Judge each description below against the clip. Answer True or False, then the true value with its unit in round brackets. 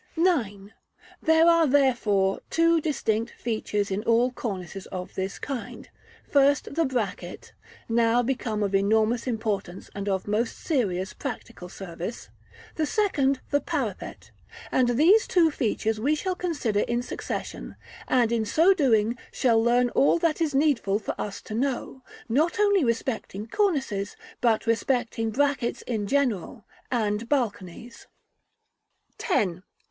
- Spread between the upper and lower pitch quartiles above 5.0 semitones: True (5.4 semitones)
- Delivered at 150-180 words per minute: False (135 wpm)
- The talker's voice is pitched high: True (235 Hz)